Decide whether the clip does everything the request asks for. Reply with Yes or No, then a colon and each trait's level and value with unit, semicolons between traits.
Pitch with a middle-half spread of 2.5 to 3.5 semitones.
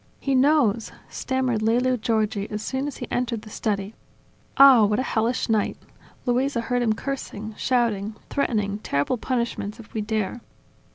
Yes: average, 3.2 semitones